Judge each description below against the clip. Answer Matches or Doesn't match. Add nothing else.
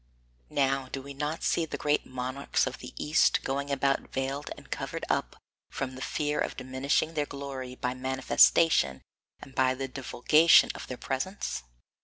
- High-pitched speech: Doesn't match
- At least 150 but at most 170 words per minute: Matches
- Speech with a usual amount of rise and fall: Doesn't match